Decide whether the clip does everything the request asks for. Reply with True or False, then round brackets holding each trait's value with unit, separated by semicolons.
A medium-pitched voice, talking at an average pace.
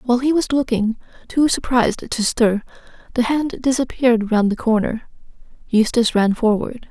False (240 Hz; 150 wpm)